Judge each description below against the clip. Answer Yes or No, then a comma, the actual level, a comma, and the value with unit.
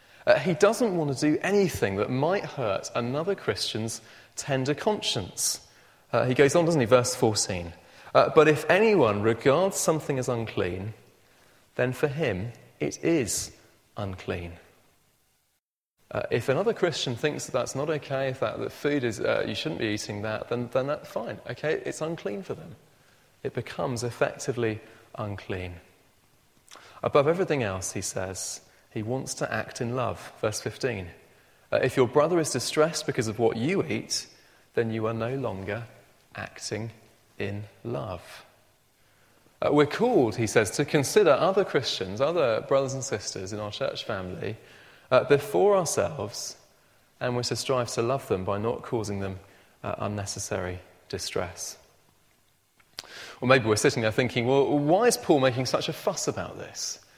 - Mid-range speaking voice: No, low, 120 Hz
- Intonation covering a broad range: Yes, wide, 5.9 semitones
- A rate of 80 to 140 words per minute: No, average, 160 wpm